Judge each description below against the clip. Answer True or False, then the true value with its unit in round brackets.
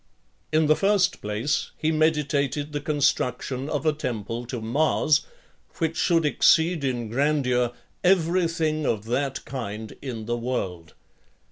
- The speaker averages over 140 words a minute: False (135 wpm)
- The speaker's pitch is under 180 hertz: True (140 Hz)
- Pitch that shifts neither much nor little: True (4.6 semitones)